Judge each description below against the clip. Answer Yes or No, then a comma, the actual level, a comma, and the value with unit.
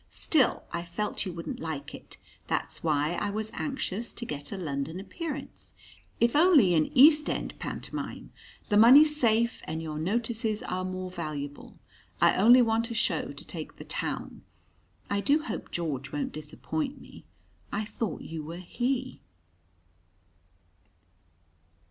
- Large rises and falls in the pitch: Yes, wide, 6.9 semitones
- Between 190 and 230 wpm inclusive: No, average, 145 wpm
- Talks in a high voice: Yes, high, 205 Hz